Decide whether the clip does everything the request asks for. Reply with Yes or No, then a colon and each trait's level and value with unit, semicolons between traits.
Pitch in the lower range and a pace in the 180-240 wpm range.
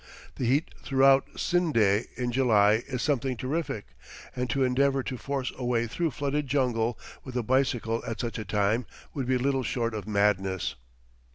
No: low, 125 Hz; average, 170 wpm